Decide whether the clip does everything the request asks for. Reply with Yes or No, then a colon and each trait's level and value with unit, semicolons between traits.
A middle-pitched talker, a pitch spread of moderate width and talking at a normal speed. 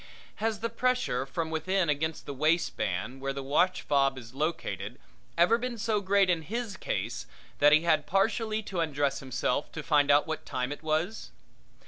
No: medium, 160 Hz; wide, 6.0 semitones; average, 170 wpm